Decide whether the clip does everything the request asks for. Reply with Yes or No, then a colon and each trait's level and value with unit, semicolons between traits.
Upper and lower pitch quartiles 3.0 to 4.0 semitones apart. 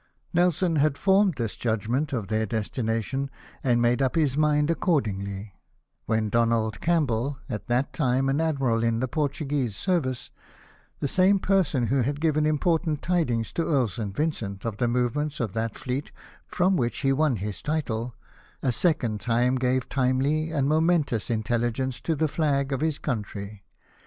No: average, 4.9 semitones